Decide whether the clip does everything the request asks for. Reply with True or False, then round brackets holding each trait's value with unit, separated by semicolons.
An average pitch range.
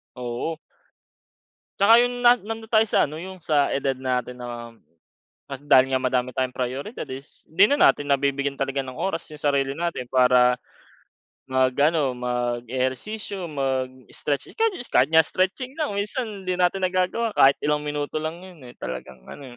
False (6.5 semitones)